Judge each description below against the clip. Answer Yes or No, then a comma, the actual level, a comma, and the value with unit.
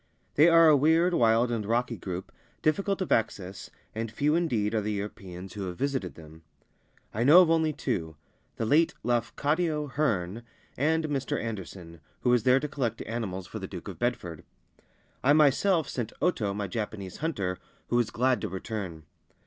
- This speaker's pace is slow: No, average, 175 wpm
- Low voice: Yes, low, 115 Hz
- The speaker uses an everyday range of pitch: No, wide, 7.1 semitones